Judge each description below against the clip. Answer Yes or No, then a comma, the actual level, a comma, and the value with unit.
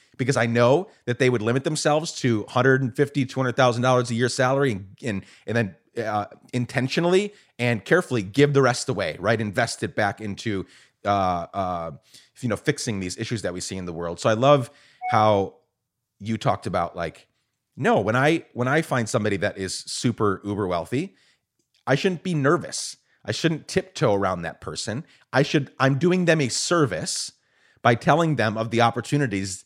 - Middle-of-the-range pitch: No, low, 120 Hz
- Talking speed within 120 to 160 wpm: No, average, 175 wpm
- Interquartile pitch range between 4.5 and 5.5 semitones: Yes, average, 5.1 semitones